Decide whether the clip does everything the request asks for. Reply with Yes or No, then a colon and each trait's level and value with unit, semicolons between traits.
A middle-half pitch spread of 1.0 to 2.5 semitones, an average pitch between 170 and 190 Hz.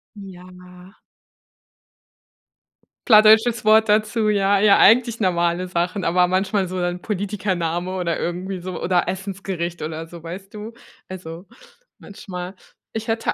No: average, 2.9 semitones; medium, 185 Hz